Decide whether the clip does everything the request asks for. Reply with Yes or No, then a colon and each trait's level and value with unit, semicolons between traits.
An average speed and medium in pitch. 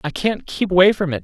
No: fast, 290 wpm; medium, 180 Hz